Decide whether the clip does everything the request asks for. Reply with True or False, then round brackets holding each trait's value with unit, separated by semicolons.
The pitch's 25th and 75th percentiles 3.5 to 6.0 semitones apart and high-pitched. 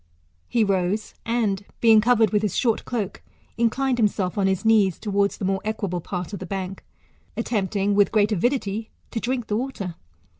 False (2.8 semitones; 210 Hz)